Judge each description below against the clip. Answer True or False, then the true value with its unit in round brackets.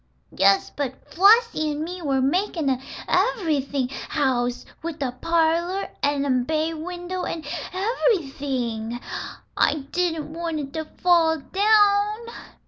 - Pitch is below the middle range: False (320 Hz)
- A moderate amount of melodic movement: True (4.7 semitones)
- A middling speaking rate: False (125 wpm)